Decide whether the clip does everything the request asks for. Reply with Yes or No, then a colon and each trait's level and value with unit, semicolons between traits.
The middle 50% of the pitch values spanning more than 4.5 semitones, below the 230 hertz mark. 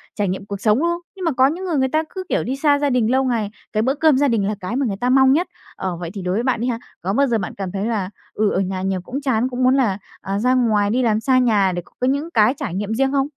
No: average, 5.0 semitones; high, 240 Hz